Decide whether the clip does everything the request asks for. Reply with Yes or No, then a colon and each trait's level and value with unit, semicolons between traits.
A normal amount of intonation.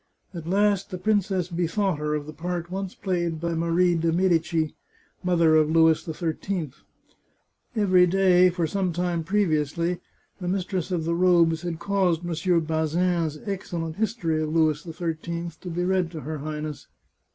No: narrow, 2.2 semitones